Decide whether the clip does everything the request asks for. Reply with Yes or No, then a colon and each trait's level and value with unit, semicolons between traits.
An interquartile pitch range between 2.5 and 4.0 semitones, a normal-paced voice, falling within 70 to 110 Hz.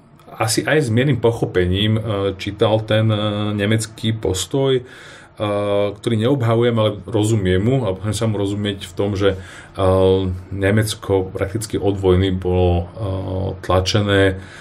Yes: average, 2.8 semitones; average, 130 wpm; low, 100 Hz